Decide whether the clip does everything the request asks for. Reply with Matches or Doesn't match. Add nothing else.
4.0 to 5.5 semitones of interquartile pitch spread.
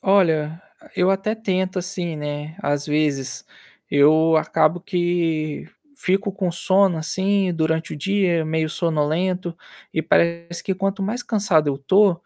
Doesn't match